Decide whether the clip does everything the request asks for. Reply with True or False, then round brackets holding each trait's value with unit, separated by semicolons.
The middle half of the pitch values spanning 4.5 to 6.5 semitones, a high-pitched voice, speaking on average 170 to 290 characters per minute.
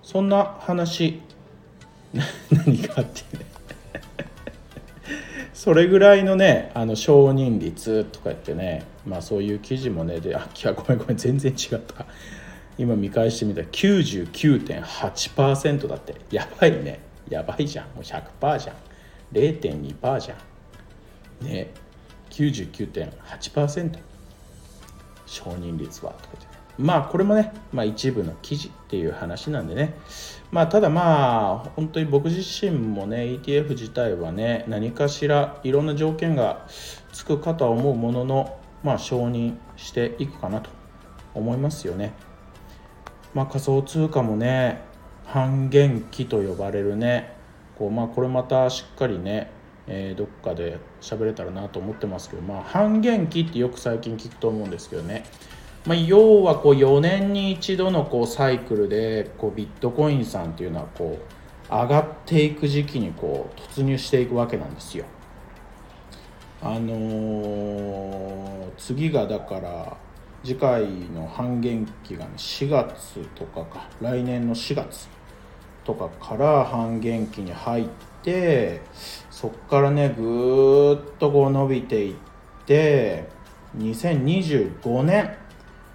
False (5.5 semitones; 125 Hz; 250 characters per minute)